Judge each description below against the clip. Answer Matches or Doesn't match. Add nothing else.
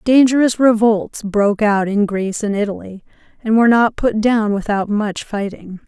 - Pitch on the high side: Matches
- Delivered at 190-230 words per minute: Doesn't match